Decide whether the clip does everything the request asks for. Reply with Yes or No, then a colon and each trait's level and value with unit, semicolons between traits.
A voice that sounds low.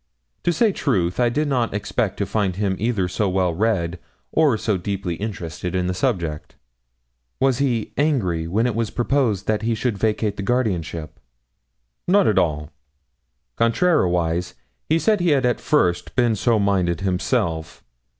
Yes: low, 105 Hz